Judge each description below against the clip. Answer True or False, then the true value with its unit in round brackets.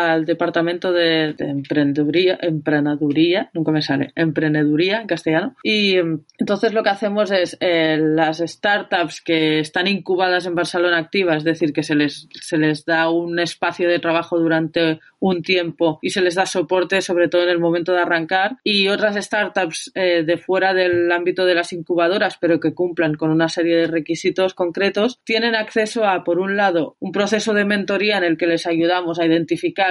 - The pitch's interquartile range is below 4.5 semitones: True (2.5 semitones)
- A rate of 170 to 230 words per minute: True (180 wpm)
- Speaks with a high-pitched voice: False (175 Hz)